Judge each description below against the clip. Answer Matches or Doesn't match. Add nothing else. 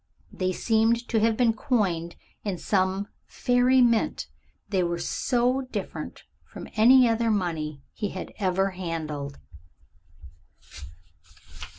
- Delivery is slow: Matches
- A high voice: Matches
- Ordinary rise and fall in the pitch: Matches